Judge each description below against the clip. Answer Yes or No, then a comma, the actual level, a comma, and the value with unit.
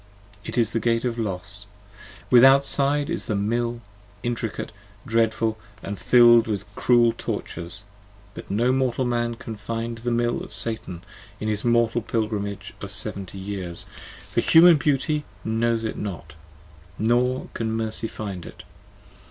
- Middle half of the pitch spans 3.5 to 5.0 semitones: No, average, 2.7 semitones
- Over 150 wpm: No, average, 145 wpm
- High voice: No, low, 115 Hz